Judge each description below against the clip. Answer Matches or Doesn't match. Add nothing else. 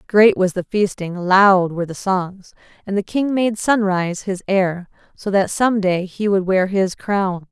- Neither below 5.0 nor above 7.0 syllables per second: Doesn't match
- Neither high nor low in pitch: Doesn't match